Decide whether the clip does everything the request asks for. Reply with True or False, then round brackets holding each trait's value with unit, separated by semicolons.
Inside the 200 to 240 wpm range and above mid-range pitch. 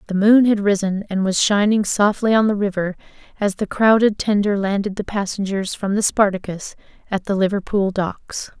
False (175 wpm; 200 Hz)